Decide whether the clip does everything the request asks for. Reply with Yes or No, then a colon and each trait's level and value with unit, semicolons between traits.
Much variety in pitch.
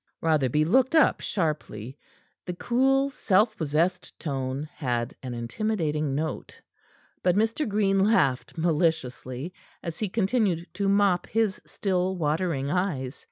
Yes: wide, 5.8 semitones